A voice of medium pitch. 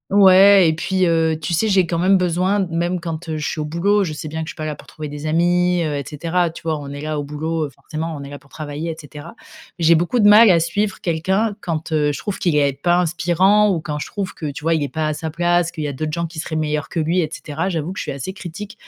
Yes: medium, 165 Hz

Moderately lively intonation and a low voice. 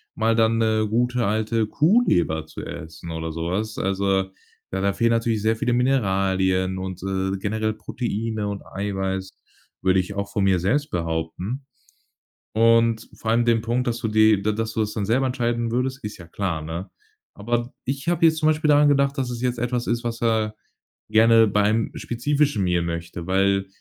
Yes: average, 3.8 semitones; low, 110 Hz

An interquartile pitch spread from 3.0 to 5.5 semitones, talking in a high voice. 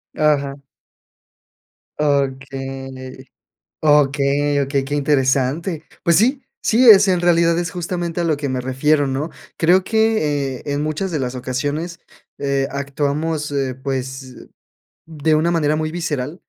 No: average, 3.4 semitones; medium, 145 Hz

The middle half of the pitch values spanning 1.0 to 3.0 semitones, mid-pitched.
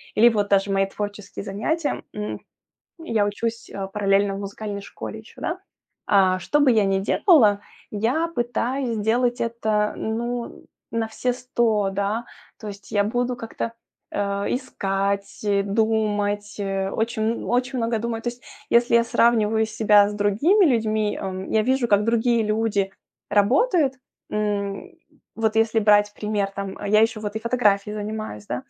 No: narrow, 2.5 semitones; high, 215 Hz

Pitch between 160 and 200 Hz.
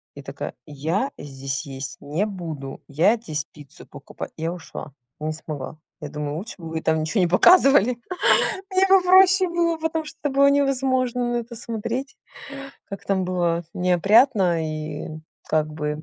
Yes: medium, 185 Hz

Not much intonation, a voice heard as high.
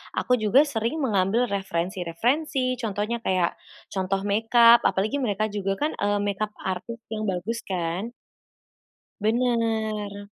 No: average, 3.2 semitones; high, 215 Hz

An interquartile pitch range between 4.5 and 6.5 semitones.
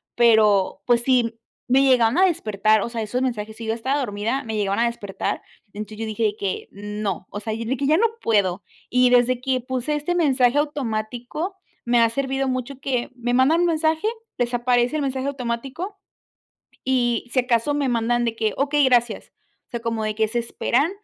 No: average, 3.3 semitones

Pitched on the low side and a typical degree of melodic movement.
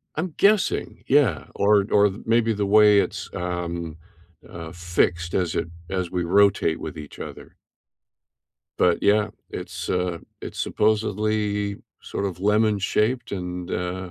Yes: low, 100 Hz; average, 3.2 semitones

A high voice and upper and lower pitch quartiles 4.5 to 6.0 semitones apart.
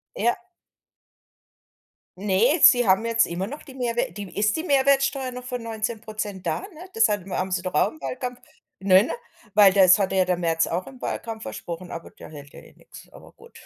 Yes: high, 210 Hz; average, 5.1 semitones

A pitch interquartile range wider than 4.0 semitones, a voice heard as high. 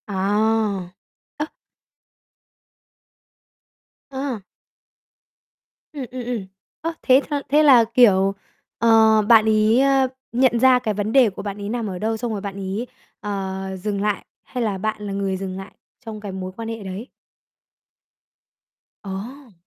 No: average, 3.7 semitones; high, 215 Hz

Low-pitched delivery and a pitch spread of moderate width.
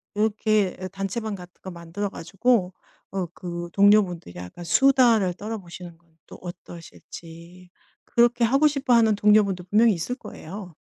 No: high, 195 Hz; average, 4.0 semitones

